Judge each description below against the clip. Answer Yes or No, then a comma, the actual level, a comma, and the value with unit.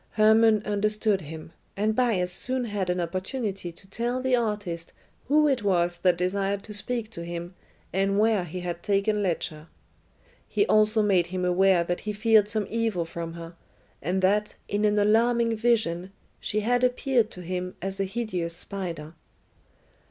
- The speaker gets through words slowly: No, average, 165 wpm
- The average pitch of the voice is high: Yes, high, 200 Hz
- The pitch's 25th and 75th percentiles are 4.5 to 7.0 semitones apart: No, average, 3.7 semitones